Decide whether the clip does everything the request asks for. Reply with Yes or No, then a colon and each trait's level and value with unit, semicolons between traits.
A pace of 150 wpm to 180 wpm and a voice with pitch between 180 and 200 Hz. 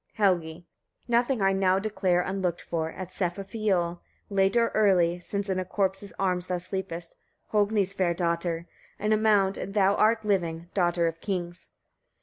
Yes: average, 160 wpm; high, 190 Hz